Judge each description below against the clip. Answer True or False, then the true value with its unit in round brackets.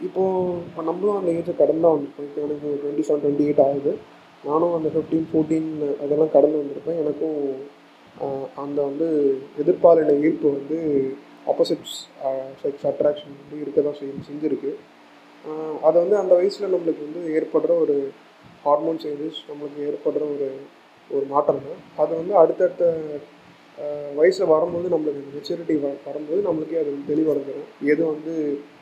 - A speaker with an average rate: False (135 wpm)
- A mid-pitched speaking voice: True (150 Hz)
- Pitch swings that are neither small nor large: False (2.1 semitones)